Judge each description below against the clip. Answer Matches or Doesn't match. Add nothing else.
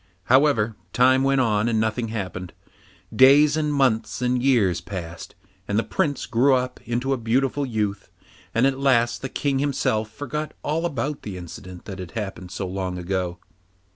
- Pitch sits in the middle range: Doesn't match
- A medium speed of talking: Matches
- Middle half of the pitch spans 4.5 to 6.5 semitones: Matches